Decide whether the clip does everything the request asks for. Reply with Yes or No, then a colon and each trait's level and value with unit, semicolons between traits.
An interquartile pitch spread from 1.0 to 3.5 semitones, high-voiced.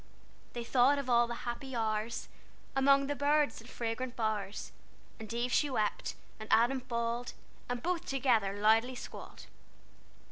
Yes: average, 3.0 semitones; high, 240 Hz